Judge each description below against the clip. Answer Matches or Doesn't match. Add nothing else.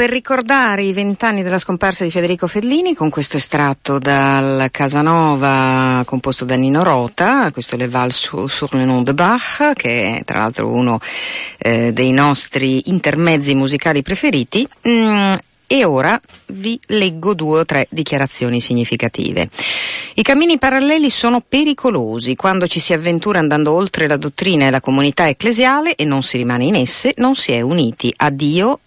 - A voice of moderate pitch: Matches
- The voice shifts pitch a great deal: Matches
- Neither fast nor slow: Matches